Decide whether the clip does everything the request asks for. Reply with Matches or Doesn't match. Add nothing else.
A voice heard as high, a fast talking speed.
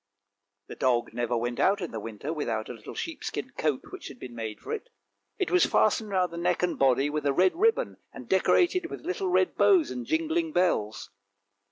Doesn't match